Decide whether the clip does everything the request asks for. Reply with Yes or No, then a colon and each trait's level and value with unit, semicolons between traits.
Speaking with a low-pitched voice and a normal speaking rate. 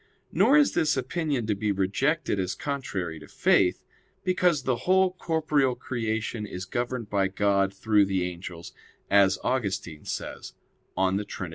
Yes: low, 105 Hz; average, 145 wpm